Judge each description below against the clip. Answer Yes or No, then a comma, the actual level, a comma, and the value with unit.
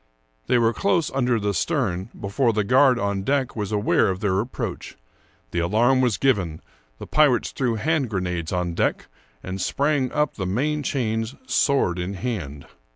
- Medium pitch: No, low, 110 Hz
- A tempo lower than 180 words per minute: Yes, average, 165 wpm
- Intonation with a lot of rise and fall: Yes, wide, 5.9 semitones